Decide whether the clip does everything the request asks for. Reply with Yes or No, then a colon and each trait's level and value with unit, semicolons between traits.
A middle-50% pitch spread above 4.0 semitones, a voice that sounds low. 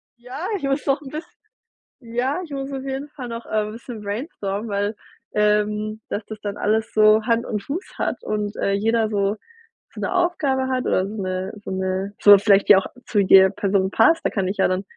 No: average, 4.7 semitones; high, 215 Hz